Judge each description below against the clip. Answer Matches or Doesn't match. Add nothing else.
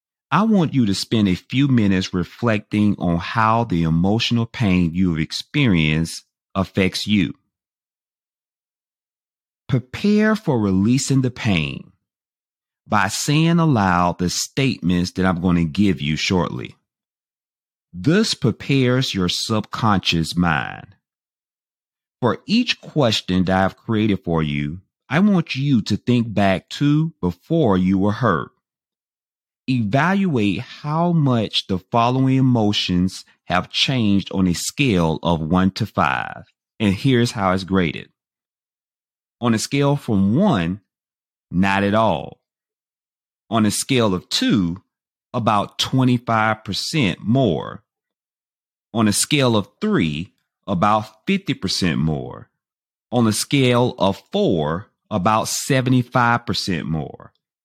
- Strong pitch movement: Matches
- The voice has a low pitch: Matches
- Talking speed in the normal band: Doesn't match